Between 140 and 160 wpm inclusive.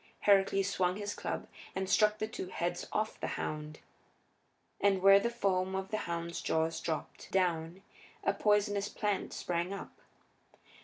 Yes: average, 150 wpm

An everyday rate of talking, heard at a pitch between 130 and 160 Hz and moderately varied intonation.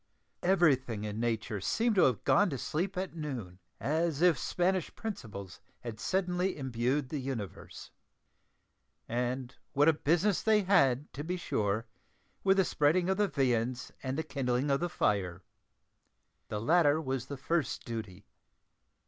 No: average, 150 wpm; medium, 140 Hz; wide, 6.9 semitones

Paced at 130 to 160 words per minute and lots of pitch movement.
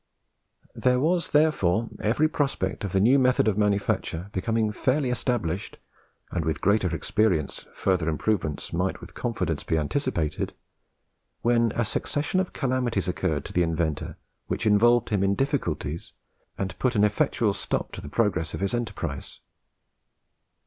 Yes: average, 145 wpm; wide, 5.7 semitones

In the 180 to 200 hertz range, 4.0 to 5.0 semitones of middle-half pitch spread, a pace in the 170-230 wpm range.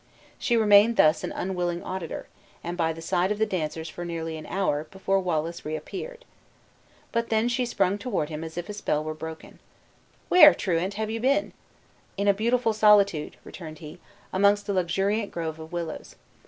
Yes: medium, 185 Hz; average, 4.6 semitones; average, 180 wpm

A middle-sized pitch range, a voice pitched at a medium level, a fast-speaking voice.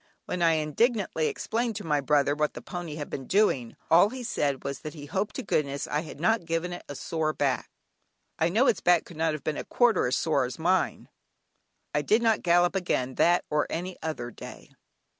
Yes: average, 4.0 semitones; medium, 160 Hz; fast, 215 wpm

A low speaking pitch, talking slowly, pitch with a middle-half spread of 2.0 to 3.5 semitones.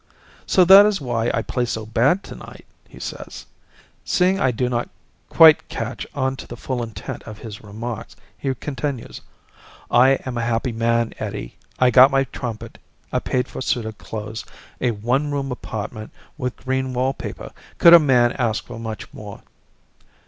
No: low, 125 Hz; average, 170 wpm; average, 2.9 semitones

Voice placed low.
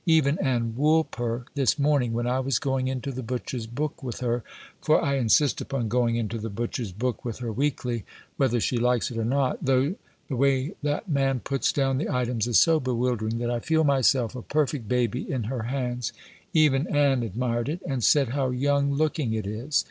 Yes: low, 125 Hz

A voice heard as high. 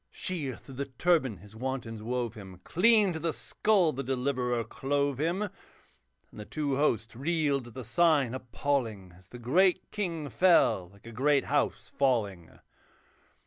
No: low, 135 Hz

